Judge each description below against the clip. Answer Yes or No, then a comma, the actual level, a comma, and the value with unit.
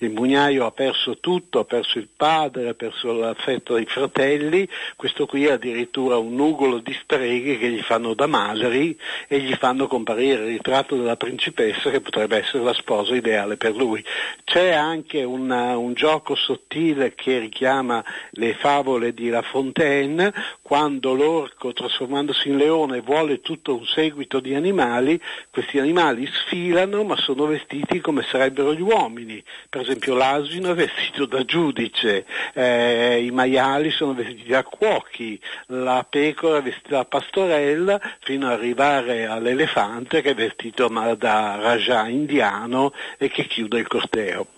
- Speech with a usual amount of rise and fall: Yes, average, 3.7 semitones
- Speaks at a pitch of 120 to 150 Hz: Yes, low, 135 Hz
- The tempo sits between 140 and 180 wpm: Yes, average, 150 wpm